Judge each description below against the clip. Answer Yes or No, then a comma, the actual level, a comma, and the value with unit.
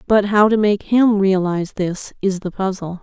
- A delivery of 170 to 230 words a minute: Yes, average, 200 wpm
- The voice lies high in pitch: Yes, high, 195 Hz